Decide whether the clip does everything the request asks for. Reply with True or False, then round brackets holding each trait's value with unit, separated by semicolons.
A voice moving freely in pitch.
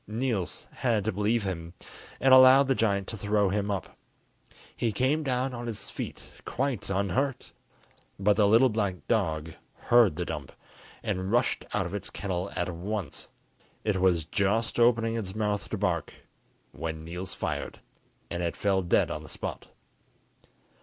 False (3.9 semitones)